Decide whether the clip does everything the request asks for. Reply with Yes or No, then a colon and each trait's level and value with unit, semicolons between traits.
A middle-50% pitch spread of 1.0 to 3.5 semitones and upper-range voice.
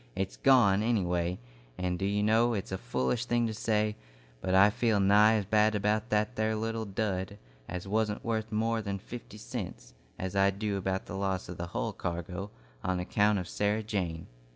No: narrow, 2.6 semitones; low, 105 Hz